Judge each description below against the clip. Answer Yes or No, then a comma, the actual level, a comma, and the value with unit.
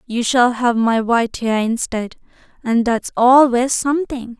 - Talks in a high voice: Yes, high, 240 Hz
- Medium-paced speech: Yes, average, 150 wpm